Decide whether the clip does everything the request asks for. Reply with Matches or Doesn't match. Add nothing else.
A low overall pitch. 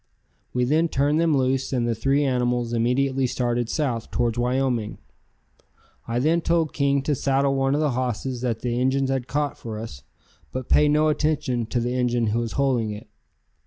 Matches